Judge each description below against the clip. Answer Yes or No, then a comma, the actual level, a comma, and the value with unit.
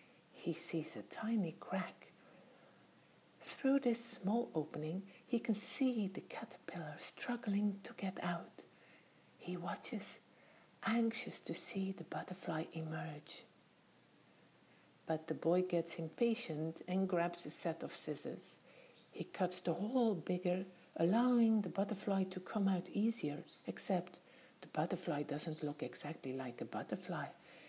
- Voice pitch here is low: No, medium, 180 Hz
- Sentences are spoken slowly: Yes, slow, 125 wpm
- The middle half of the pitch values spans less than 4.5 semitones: No, average, 5.1 semitones